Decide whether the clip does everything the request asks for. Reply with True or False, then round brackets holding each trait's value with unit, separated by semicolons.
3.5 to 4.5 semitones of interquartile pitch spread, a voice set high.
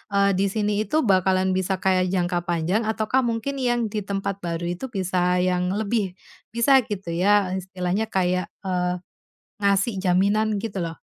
False (2.9 semitones; 195 Hz)